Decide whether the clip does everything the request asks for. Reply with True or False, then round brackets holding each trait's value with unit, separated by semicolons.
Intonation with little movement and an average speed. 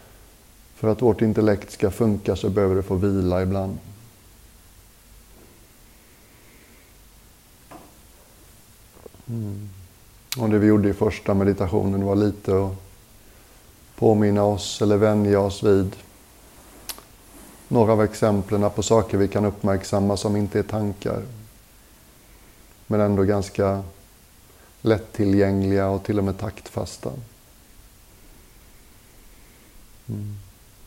False (1.7 semitones; 100 wpm)